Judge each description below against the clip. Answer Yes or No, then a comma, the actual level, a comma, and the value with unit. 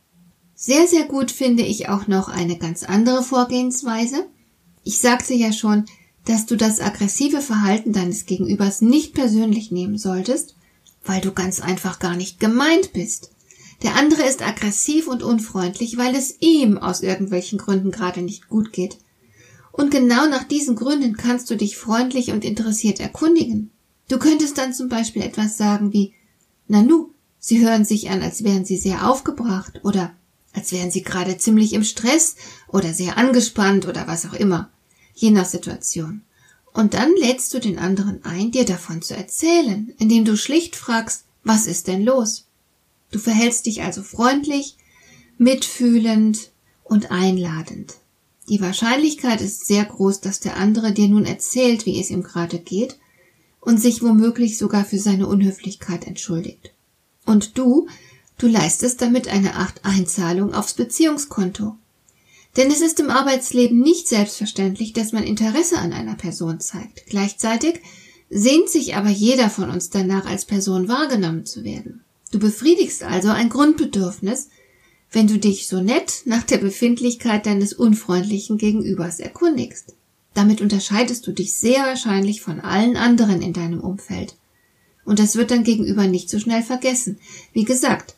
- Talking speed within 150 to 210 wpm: Yes, average, 155 wpm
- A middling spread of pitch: Yes, average, 4.3 semitones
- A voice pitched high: Yes, high, 215 Hz